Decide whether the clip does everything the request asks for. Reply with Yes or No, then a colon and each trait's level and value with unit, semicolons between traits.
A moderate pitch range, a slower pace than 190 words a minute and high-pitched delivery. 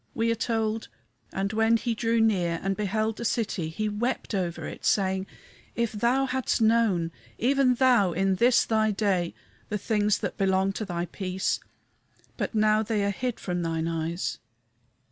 Yes: average, 3.2 semitones; average, 165 wpm; high, 210 Hz